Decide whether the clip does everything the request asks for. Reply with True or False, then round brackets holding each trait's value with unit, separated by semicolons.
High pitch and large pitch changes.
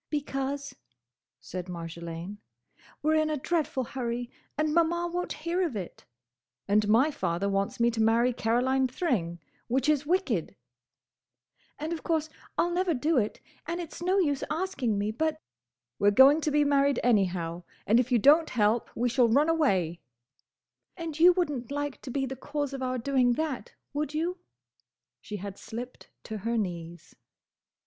True (265 Hz; 6.1 semitones)